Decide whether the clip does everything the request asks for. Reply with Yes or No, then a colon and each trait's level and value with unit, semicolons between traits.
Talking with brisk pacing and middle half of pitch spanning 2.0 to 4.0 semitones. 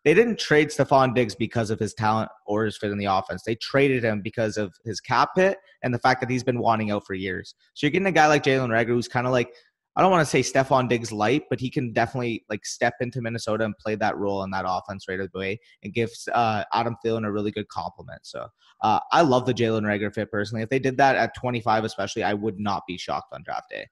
Yes: fast, 260 wpm; average, 3.4 semitones